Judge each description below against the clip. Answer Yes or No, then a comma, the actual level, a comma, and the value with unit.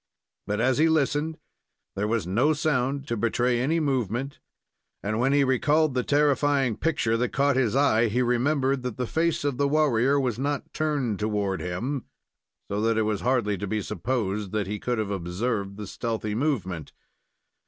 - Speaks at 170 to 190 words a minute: Yes, average, 175 wpm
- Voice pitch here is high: No, low, 125 Hz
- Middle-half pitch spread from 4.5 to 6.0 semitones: Yes, average, 5.0 semitones